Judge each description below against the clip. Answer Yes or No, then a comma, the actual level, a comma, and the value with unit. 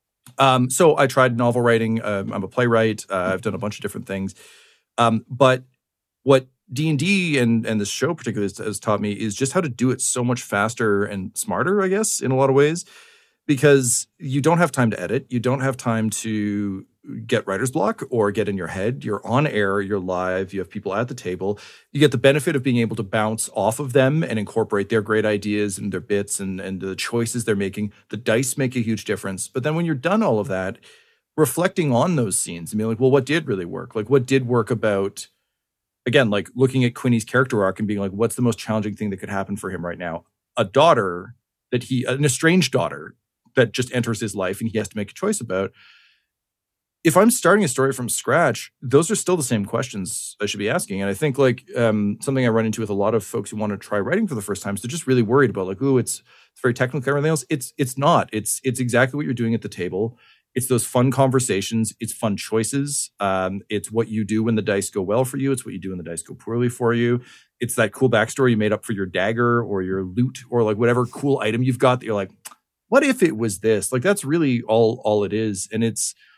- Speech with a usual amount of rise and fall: Yes, average, 4.0 semitones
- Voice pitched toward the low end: Yes, low, 115 Hz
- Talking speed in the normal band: No, fast, 245 wpm